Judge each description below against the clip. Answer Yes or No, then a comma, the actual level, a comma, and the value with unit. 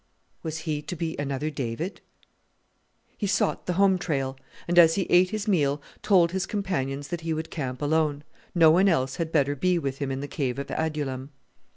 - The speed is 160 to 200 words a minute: Yes, average, 195 wpm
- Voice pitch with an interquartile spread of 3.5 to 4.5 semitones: Yes, average, 4.0 semitones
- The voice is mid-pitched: Yes, medium, 160 Hz